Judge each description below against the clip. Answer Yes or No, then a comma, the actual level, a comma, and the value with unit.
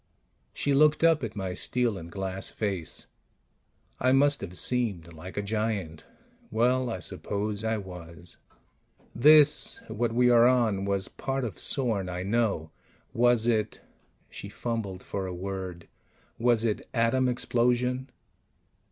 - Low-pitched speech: Yes, low, 110 Hz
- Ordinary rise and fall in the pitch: Yes, average, 4.5 semitones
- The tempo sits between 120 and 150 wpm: Yes, average, 140 wpm